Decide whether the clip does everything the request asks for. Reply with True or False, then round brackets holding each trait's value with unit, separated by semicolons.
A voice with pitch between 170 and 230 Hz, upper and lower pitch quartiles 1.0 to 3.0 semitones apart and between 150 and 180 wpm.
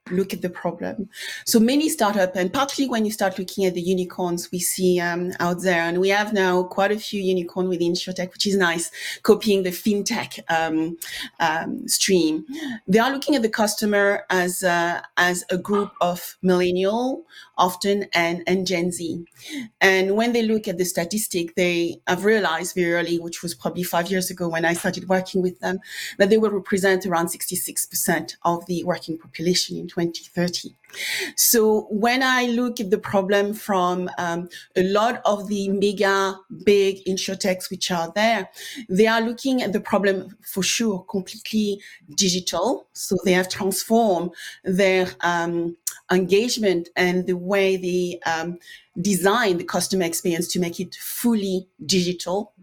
True (185 Hz; 2.7 semitones; 165 wpm)